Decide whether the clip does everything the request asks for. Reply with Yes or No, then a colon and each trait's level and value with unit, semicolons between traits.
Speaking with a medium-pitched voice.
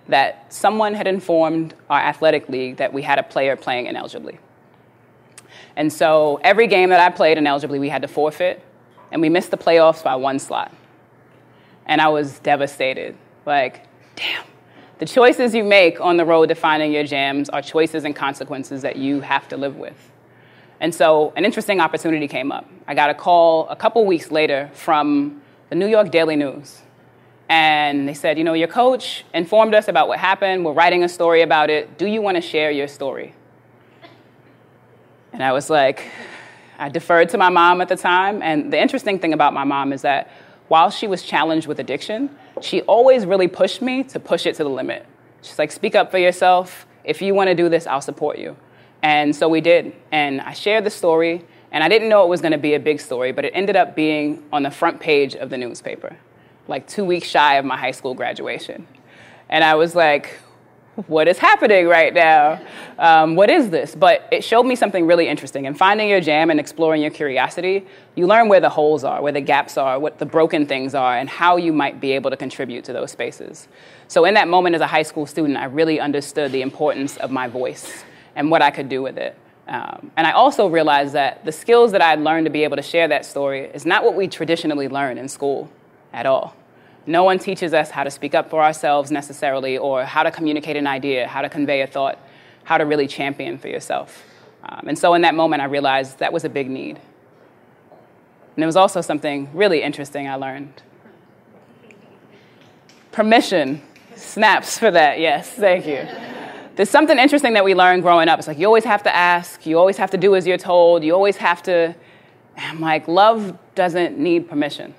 Yes: medium, 160 Hz